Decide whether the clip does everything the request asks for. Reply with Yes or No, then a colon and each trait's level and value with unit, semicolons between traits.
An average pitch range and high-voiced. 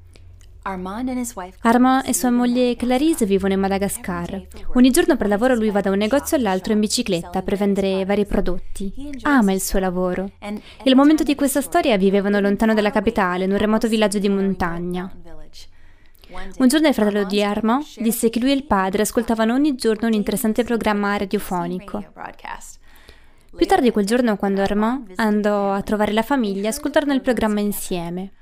Yes: average, 4.0 semitones; high, 210 Hz